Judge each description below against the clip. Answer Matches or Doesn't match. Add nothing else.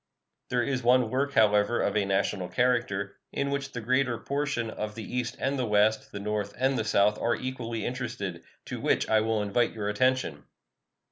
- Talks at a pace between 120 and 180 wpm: Doesn't match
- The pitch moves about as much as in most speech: Matches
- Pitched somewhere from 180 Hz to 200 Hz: Doesn't match